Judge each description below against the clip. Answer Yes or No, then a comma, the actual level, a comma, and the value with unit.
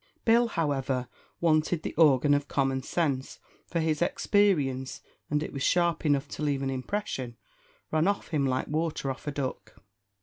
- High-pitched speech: No, medium, 145 Hz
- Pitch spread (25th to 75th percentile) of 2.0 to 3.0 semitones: No, average, 3.7 semitones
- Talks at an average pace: Yes, average, 165 wpm